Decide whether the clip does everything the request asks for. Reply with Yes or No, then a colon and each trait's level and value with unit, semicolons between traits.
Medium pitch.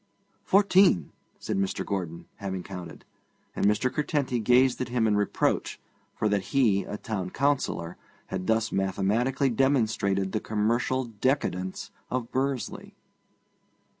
No: low, 110 Hz